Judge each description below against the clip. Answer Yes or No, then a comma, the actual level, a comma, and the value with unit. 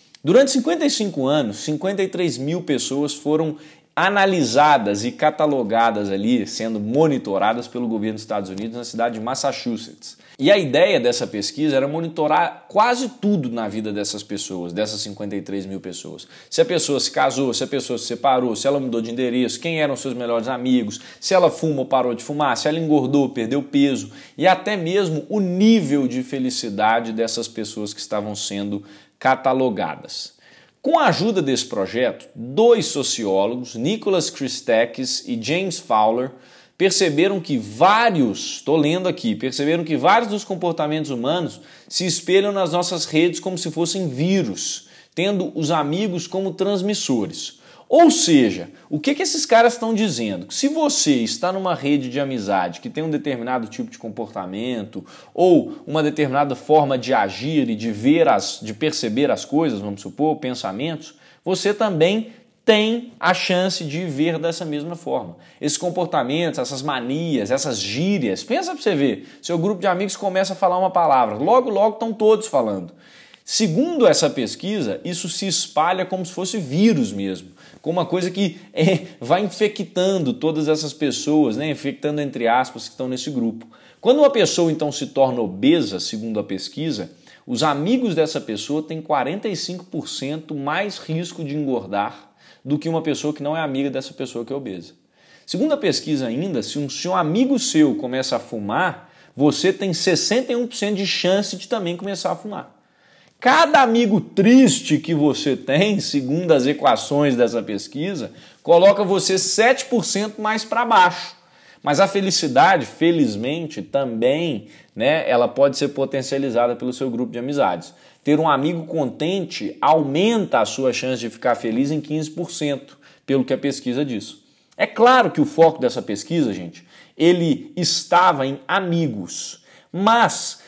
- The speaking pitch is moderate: Yes, medium, 155 Hz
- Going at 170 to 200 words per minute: No, average, 160 wpm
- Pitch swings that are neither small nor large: No, wide, 6.6 semitones